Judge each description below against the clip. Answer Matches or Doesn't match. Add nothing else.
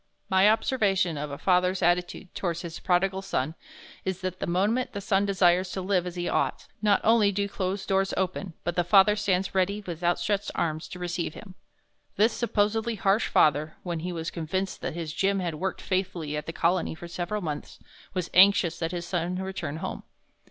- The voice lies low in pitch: Doesn't match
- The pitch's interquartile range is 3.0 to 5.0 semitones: Doesn't match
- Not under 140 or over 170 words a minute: Doesn't match